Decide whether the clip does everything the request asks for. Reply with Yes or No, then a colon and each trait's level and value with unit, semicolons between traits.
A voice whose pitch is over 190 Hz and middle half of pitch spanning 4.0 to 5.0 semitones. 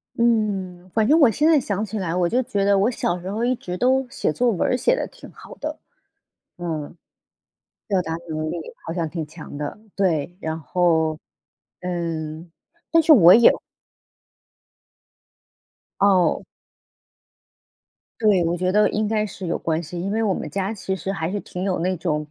No: medium, 185 Hz; average, 4.4 semitones